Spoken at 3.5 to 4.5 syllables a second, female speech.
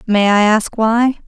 Yes: 3.8 syllables/s; female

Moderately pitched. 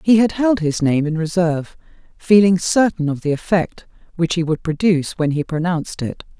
Yes: medium, 170 Hz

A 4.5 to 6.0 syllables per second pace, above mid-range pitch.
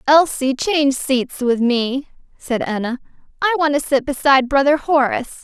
Yes: 5.0 syllables/s; very high, 275 Hz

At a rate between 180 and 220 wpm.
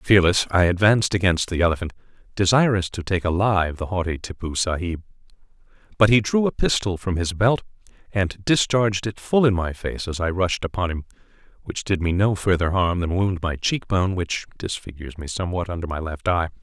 Yes: average, 190 wpm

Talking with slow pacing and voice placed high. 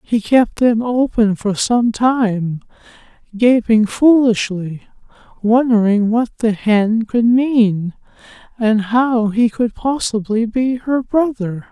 Yes: slow, 120 wpm; high, 225 Hz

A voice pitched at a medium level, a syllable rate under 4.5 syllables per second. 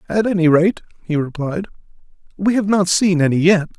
No: medium, 180 Hz; 5.3 syllables/s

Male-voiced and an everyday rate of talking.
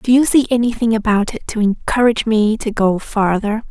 No: female; average, 195 wpm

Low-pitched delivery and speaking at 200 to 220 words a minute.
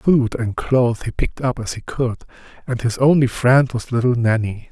Yes: low, 125 Hz; fast, 205 wpm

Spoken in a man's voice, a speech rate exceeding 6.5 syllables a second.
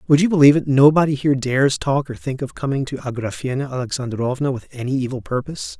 Yes: male; 6.7 syllables/s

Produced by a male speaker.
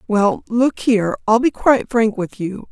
No: female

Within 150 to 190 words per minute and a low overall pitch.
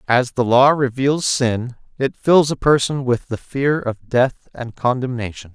Yes: average, 175 wpm; low, 125 Hz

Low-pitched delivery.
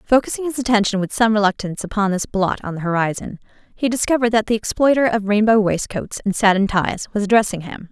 No: high, 210 Hz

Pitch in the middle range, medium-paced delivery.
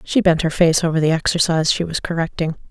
No: medium, 165 Hz; fast, 220 wpm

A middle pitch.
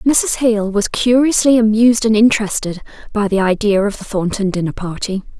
No: high, 215 Hz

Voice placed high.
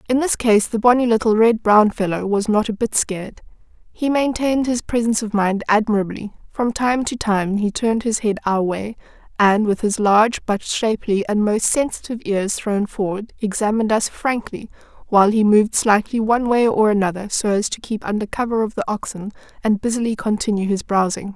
Yes: high, 215 Hz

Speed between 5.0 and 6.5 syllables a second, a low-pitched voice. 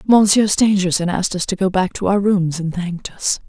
No: 5.5 syllables/s; medium, 185 Hz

